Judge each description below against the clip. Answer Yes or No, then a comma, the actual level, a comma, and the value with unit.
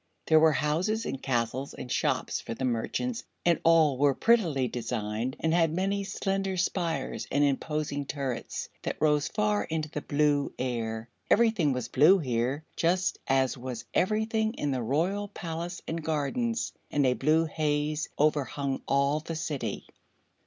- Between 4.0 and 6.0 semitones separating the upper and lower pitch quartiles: Yes, average, 4.7 semitones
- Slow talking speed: No, average, 150 wpm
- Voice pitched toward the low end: No, medium, 150 Hz